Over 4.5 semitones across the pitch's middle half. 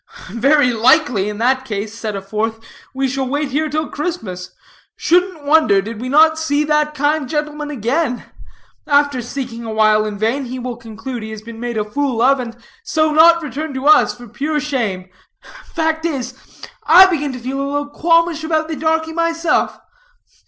Yes: average, 5.1 semitones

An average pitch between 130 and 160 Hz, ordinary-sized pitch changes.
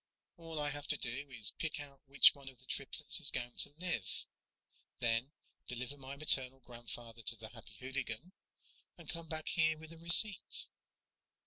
Yes: medium, 140 Hz; average, 4.7 semitones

